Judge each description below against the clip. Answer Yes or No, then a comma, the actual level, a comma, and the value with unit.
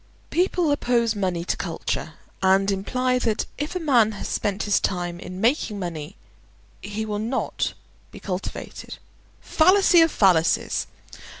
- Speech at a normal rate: No, slow, 130 wpm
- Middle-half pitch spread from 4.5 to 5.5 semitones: Yes, average, 5.1 semitones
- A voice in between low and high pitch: No, high, 210 Hz